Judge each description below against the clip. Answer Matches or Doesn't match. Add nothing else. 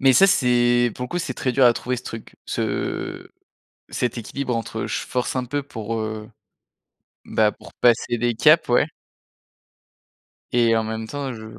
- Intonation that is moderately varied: Doesn't match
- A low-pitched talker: Matches